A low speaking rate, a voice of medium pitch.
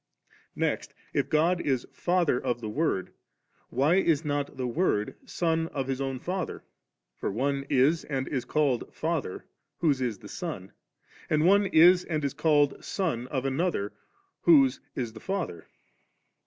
No: average, 150 wpm; medium, 145 Hz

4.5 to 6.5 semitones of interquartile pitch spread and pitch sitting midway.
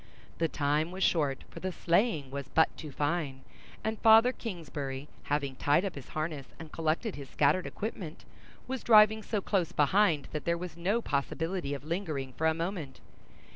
Yes: average, 4.9 semitones; medium, 165 Hz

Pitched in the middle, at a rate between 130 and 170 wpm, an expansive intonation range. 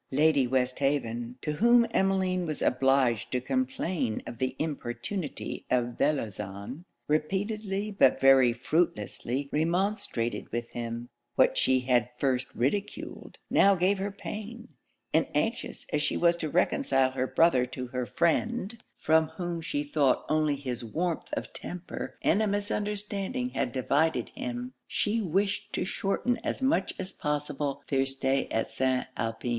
Yes: medium, 150 Hz; average, 145 wpm; wide, 7.1 semitones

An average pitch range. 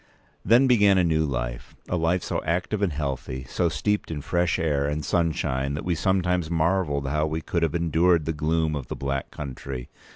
Yes: average, 3.8 semitones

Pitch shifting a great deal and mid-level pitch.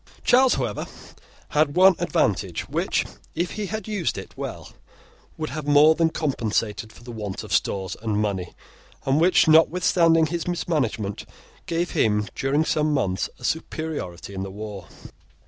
Yes: wide, 7.8 semitones; medium, 150 Hz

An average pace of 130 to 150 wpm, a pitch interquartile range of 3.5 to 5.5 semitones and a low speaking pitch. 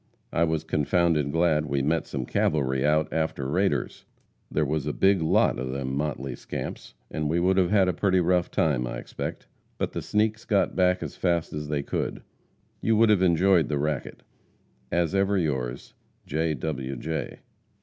No: average, 180 wpm; average, 4.1 semitones; very low, 80 Hz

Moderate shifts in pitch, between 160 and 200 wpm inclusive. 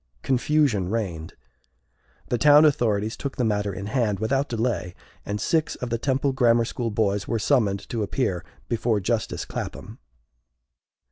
No: average, 4.1 semitones; average, 145 wpm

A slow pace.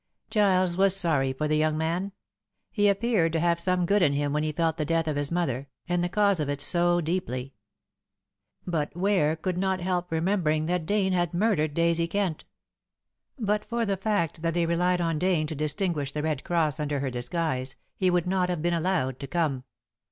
No: average, 200 wpm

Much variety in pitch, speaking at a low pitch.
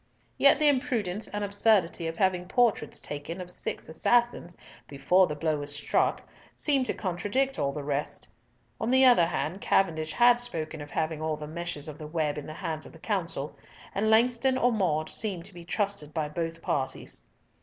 No: wide, 5.9 semitones; medium, 175 Hz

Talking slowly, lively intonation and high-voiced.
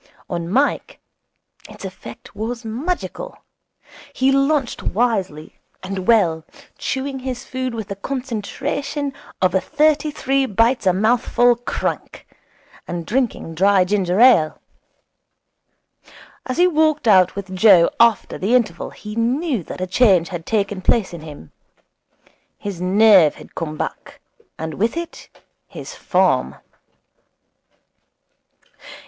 Yes: slow, 120 wpm; wide, 6.0 semitones; high, 220 Hz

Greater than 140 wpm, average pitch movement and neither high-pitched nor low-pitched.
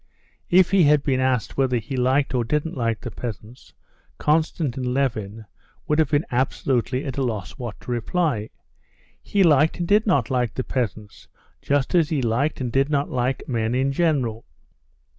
No: average, 175 wpm; average, 3.9 semitones; low, 130 Hz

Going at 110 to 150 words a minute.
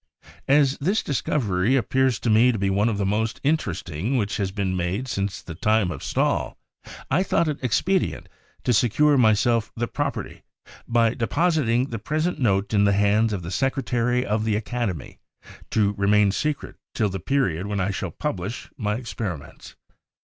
No: average, 175 wpm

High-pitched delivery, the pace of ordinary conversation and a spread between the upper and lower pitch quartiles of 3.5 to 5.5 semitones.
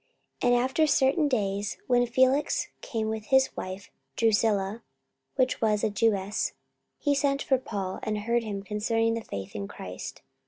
Yes: high, 225 Hz; average, 160 wpm; average, 4.0 semitones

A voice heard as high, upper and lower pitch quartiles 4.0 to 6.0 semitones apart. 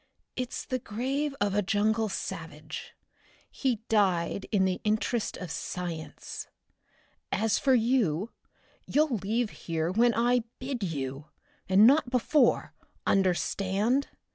Yes: high, 215 Hz; average, 4.8 semitones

